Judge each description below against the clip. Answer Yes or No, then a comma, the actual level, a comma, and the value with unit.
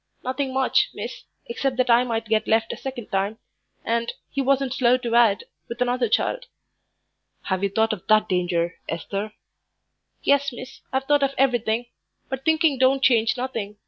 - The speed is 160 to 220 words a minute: Yes, average, 170 wpm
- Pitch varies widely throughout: No, average, 3.4 semitones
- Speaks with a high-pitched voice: Yes, high, 245 Hz